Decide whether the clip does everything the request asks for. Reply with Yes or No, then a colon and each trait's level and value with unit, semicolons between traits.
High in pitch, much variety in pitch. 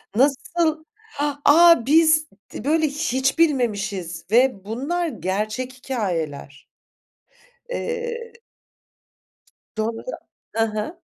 Yes: very high, 265 Hz; wide, 7.1 semitones